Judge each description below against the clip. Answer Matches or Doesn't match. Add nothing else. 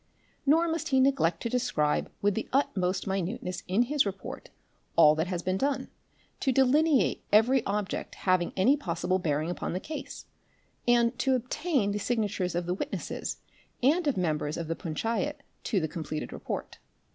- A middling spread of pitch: Doesn't match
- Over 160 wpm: Matches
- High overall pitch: Matches